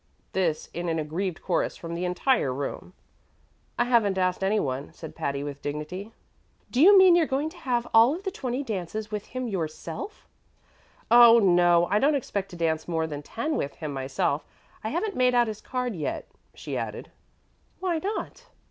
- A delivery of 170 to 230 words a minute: Yes, average, 185 wpm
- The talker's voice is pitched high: Yes, high, 200 Hz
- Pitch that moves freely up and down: Yes, wide, 7.7 semitones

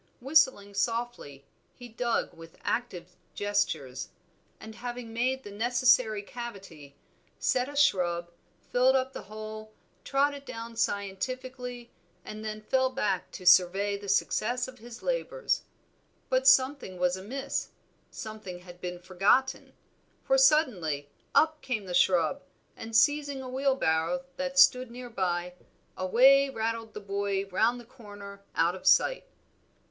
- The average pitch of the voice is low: No, high, 225 Hz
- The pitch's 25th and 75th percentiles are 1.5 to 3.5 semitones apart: No, average, 5.2 semitones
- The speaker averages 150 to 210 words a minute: No, slow, 135 wpm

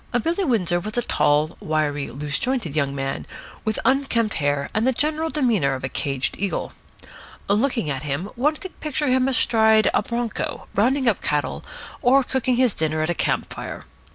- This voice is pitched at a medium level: No, high, 215 Hz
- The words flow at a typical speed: Yes, average, 180 wpm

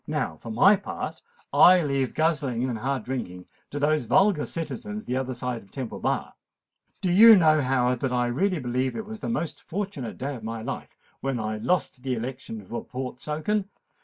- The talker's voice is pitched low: Yes, low, 130 Hz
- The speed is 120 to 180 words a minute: No, average, 190 wpm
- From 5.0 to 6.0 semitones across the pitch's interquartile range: Yes, wide, 5.4 semitones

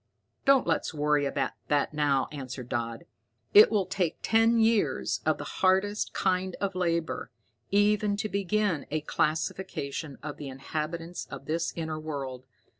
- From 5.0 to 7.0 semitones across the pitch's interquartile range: Yes, wide, 5.4 semitones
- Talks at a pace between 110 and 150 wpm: Yes, average, 145 wpm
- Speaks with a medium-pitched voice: Yes, medium, 165 Hz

